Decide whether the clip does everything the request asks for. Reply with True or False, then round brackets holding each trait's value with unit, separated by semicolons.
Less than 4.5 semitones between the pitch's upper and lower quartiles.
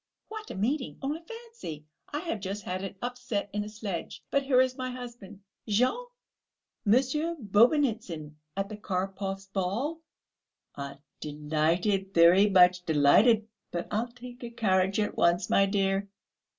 False (5.1 semitones)